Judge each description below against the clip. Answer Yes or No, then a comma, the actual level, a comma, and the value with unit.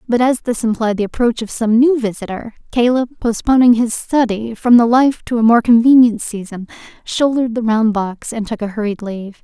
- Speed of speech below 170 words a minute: No, average, 195 wpm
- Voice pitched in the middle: No, high, 230 Hz